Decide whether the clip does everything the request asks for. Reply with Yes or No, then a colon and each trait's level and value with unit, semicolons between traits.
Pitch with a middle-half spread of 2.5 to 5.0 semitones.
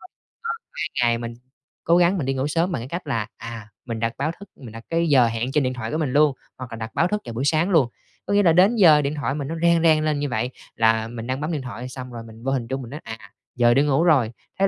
No: wide, 5.4 semitones